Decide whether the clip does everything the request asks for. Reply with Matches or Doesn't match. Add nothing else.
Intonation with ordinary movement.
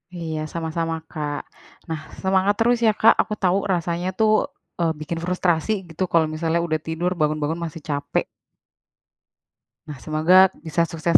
Doesn't match